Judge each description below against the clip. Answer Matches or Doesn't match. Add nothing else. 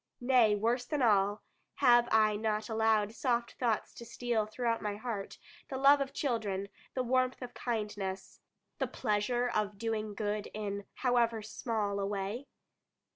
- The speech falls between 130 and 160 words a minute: Matches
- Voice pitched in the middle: Doesn't match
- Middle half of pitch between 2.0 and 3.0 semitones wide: Matches